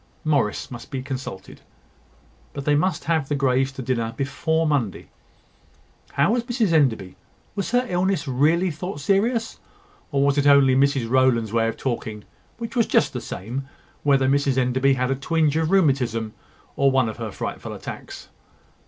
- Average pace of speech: Yes, average, 165 wpm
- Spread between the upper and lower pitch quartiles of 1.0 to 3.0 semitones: No, average, 4.1 semitones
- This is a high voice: No, medium, 140 Hz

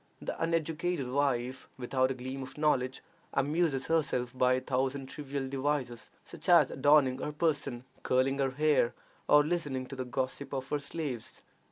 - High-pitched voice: No, low, 135 Hz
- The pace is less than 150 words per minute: No, average, 160 wpm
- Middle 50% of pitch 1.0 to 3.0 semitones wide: Yes, narrow, 2.5 semitones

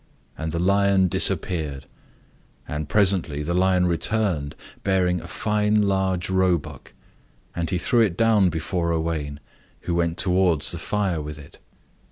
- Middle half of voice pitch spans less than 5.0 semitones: Yes, average, 3.0 semitones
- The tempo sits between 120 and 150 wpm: Yes, average, 140 wpm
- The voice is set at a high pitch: No, very low, 90 Hz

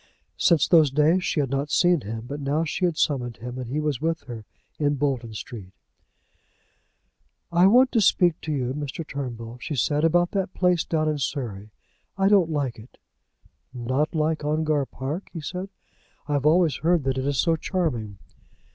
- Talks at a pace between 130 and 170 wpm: No, average, 180 wpm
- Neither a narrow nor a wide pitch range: Yes, average, 4.3 semitones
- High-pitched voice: No, medium, 150 Hz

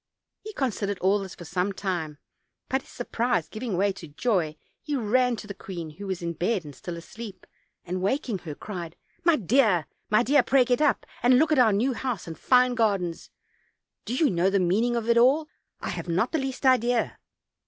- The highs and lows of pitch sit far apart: Yes, wide, 5.7 semitones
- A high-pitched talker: Yes, high, 210 Hz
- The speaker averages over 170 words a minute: Yes, fast, 205 wpm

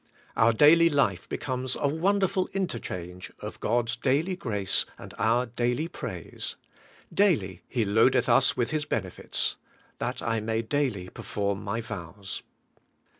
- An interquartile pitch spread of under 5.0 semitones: No, wide, 5.5 semitones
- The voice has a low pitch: Yes, low, 120 Hz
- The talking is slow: Yes, slow, 130 wpm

